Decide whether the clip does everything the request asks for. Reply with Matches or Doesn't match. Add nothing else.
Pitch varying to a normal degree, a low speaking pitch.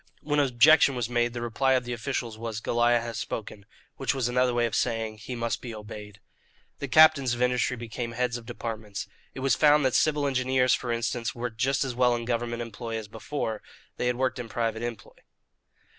Doesn't match